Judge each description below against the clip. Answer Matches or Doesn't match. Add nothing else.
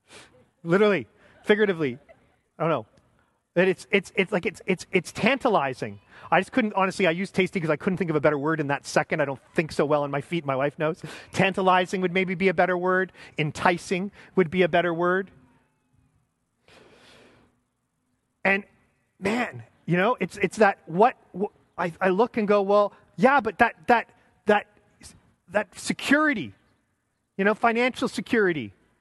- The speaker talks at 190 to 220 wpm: Doesn't match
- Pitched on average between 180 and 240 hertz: Matches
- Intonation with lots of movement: Doesn't match